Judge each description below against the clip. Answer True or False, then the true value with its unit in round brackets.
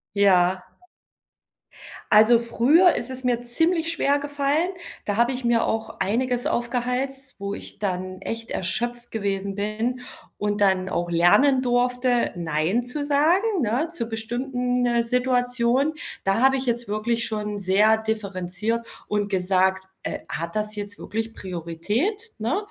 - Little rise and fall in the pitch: False (4.0 semitones)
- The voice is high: True (235 Hz)